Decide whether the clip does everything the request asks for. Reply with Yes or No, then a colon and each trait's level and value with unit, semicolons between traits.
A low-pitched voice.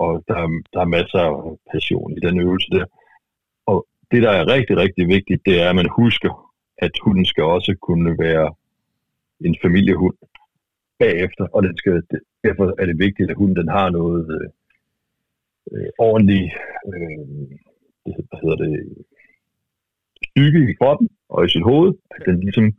Yes: very low, 90 Hz